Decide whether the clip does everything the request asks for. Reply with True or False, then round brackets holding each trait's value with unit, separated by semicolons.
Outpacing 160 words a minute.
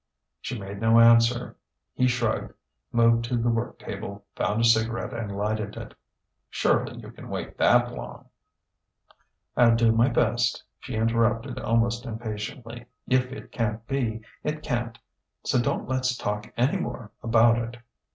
False (150 wpm)